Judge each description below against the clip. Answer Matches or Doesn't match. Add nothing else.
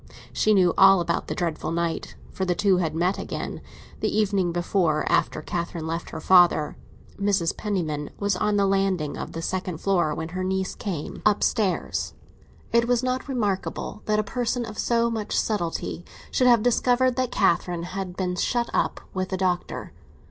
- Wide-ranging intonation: Doesn't match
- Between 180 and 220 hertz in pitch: Matches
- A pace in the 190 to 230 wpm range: Doesn't match